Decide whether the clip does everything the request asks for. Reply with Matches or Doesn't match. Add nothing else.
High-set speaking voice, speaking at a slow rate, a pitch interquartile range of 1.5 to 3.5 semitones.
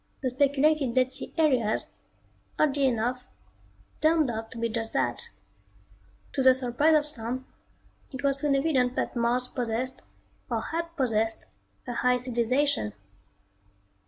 Matches